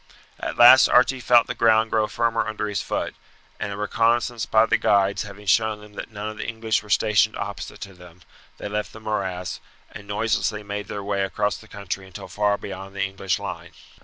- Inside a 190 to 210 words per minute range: Yes, fast, 205 wpm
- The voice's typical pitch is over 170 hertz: No, low, 105 Hz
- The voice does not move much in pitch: Yes, narrow, 1.9 semitones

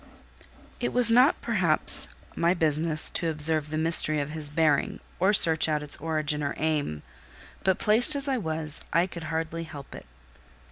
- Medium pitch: Yes, medium, 160 Hz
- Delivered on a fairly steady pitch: Yes, narrow, 2.3 semitones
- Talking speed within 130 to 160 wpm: No, average, 170 wpm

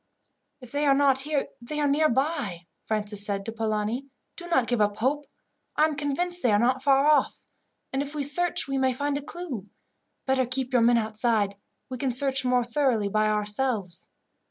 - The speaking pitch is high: Yes, very high, 260 Hz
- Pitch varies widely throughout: No, average, 4.5 semitones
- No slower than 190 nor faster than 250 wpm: Yes, average, 195 wpm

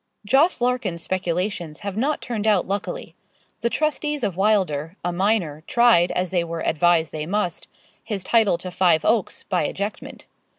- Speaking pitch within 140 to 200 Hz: Yes, high, 190 Hz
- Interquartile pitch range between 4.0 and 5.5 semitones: Yes, average, 4.4 semitones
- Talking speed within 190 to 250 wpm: No, average, 160 wpm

